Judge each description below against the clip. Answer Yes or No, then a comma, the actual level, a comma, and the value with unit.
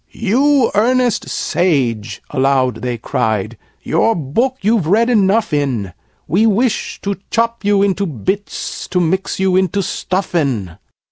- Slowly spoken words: Yes, slow, 130 wpm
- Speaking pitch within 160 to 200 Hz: Yes, high, 190 Hz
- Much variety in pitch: Yes, wide, 8.3 semitones